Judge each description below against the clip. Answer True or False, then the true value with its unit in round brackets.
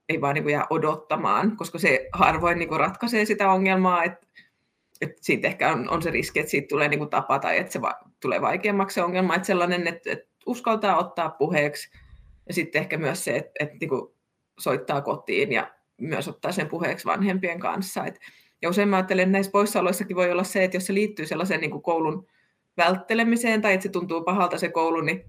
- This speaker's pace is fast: True (175 wpm)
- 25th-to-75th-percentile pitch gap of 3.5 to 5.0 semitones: False (2.8 semitones)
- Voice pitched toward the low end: False (180 Hz)